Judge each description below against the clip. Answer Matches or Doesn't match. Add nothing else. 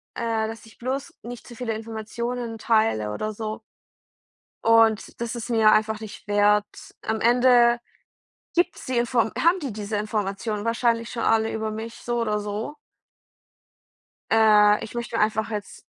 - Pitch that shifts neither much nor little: Doesn't match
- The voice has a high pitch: Matches